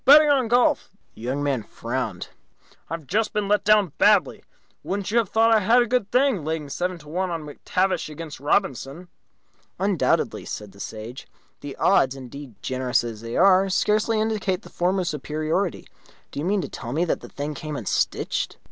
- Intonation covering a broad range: Yes, wide, 6.8 semitones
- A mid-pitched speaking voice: Yes, medium, 175 Hz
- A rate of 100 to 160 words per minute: No, average, 185 wpm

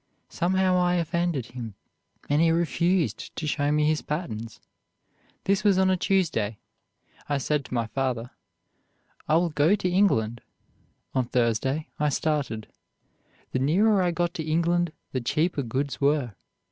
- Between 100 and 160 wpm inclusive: Yes, average, 145 wpm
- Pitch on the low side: No, medium, 150 Hz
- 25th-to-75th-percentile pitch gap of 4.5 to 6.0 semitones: Yes, average, 5.2 semitones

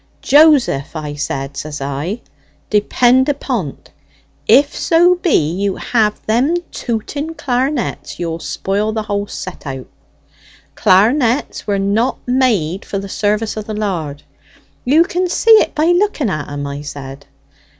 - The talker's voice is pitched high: Yes, high, 215 Hz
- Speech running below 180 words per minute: Yes, average, 140 wpm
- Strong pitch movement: Yes, wide, 8.6 semitones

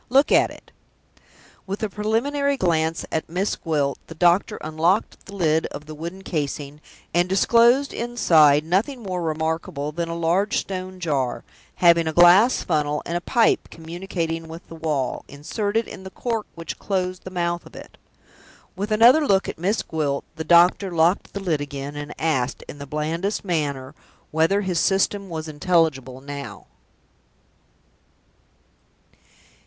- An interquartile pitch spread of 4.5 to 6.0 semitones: No, average, 4.0 semitones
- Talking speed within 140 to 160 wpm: Yes, average, 150 wpm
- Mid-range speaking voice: Yes, medium, 170 Hz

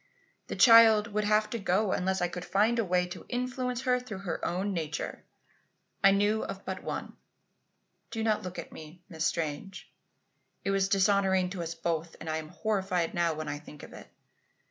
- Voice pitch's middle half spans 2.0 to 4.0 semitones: Yes, average, 3.7 semitones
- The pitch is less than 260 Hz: Yes, high, 190 Hz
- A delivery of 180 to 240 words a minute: Yes, average, 190 wpm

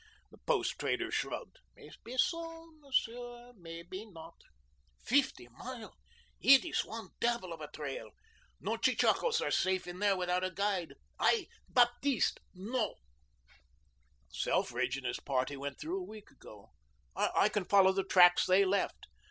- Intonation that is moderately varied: No, wide, 6.1 semitones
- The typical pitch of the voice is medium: No, high, 200 Hz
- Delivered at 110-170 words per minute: Yes, average, 140 wpm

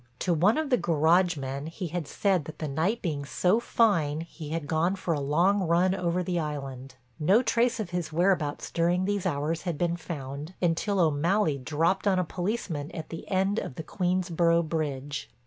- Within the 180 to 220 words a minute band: Yes, average, 190 wpm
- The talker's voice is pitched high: No, medium, 170 Hz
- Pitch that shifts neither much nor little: Yes, average, 3.7 semitones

